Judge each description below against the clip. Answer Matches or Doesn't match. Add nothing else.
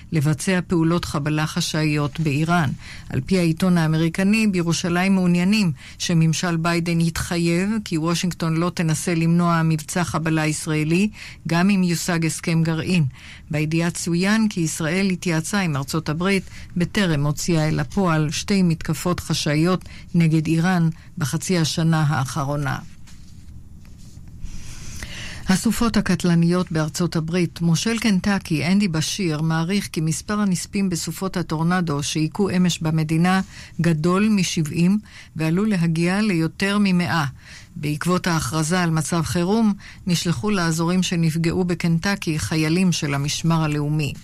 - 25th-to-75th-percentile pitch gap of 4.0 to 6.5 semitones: Doesn't match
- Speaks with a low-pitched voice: Doesn't match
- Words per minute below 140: Matches